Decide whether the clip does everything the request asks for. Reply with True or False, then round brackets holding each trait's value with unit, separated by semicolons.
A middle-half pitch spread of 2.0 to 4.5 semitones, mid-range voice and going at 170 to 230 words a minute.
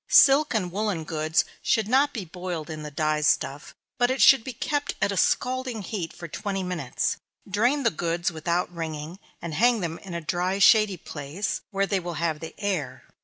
False (5.2 semitones; 180 Hz; 195 wpm)